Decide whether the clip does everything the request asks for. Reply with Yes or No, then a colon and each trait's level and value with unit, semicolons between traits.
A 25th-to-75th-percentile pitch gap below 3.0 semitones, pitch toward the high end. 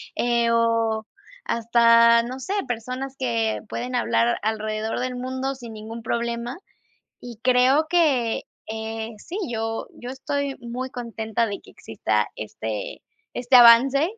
Yes: narrow, 2.4 semitones; high, 235 Hz